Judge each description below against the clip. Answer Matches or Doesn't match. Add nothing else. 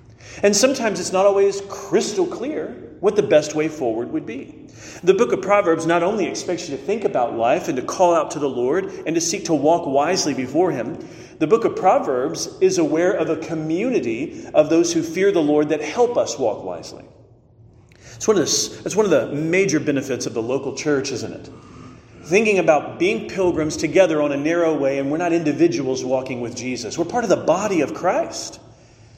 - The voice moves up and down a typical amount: Doesn't match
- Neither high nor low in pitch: Matches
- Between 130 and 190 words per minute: Doesn't match